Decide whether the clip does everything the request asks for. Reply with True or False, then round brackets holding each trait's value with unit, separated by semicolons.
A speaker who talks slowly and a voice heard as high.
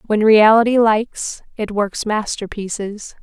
True (110 wpm; 215 Hz)